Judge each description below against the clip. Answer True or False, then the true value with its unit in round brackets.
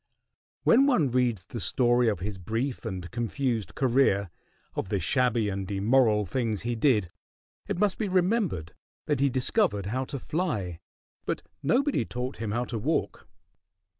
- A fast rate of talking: False (155 wpm)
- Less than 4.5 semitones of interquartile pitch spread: False (5.3 semitones)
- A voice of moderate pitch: False (120 Hz)